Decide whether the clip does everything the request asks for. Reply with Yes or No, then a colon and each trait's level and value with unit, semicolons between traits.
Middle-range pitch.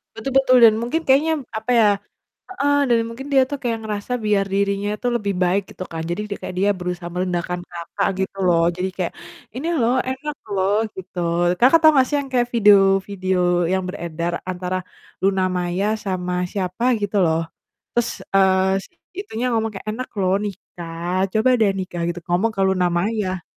No: high, 195 Hz